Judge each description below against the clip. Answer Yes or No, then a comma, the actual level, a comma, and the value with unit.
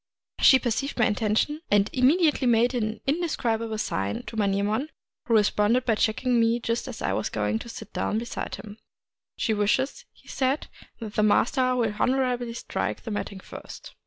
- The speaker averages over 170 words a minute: Yes, average, 180 wpm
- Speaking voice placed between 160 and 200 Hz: No, high, 230 Hz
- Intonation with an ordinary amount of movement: Yes, average, 3.1 semitones